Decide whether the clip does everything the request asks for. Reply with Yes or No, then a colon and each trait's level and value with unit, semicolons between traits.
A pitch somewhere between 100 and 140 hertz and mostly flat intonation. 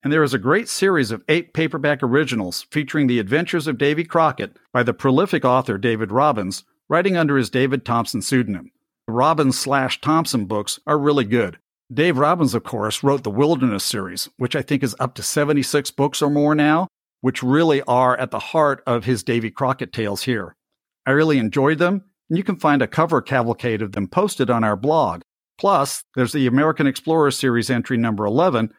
No: low, 135 Hz; average, 3.8 semitones